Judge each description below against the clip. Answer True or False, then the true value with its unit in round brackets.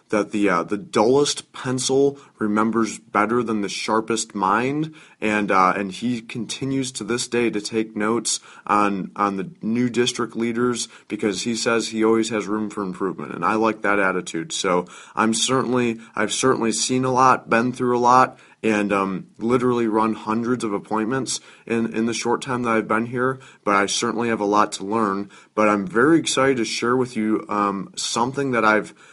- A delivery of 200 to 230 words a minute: False (185 wpm)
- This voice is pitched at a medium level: False (115 Hz)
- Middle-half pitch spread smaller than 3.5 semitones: True (2.7 semitones)